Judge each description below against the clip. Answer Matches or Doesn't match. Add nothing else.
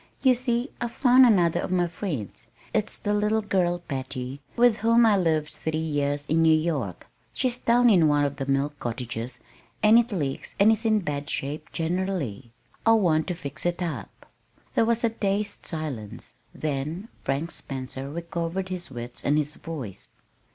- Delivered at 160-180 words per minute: Matches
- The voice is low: Doesn't match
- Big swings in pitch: Matches